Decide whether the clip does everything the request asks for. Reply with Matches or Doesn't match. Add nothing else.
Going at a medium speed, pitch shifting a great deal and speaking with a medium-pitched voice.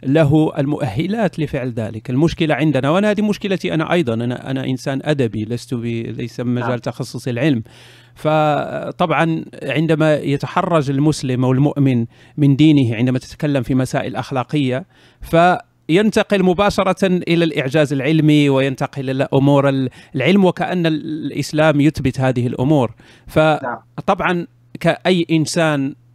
Doesn't match